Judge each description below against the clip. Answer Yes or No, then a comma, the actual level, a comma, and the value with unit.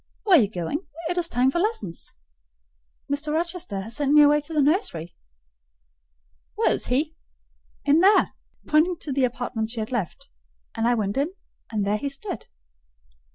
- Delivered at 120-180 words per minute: Yes, average, 170 wpm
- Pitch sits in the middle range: No, very high, 280 Hz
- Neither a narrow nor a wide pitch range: No, wide, 6.2 semitones